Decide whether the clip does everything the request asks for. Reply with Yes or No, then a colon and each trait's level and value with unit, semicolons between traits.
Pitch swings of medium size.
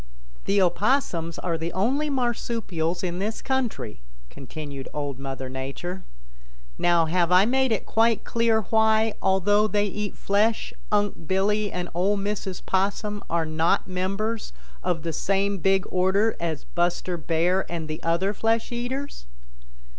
Yes: average, 4.2 semitones